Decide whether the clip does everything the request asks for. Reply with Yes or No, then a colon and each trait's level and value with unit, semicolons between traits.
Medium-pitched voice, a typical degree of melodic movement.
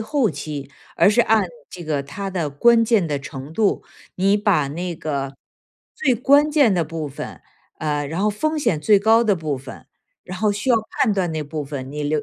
No: medium, 180 Hz; wide, 6.5 semitones